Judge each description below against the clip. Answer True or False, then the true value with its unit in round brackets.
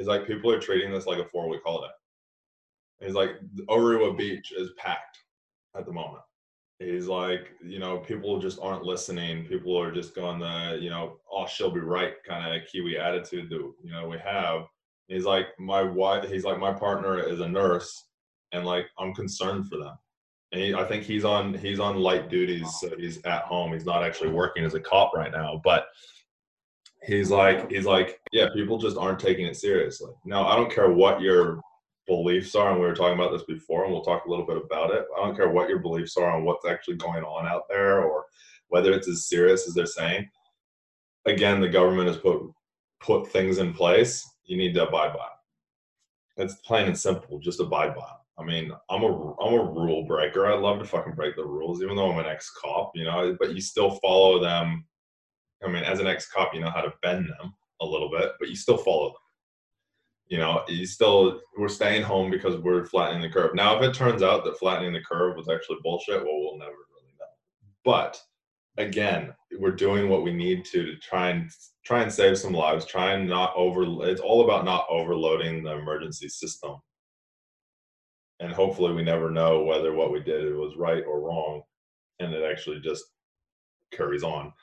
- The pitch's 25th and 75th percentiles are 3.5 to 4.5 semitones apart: True (4.0 semitones)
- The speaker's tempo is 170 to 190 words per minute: False (205 wpm)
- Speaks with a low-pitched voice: True (95 Hz)